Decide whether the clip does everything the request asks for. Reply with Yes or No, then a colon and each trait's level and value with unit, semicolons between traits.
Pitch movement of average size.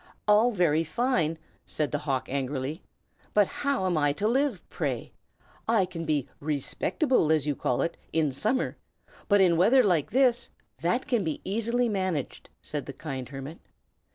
No: wide, 7.2 semitones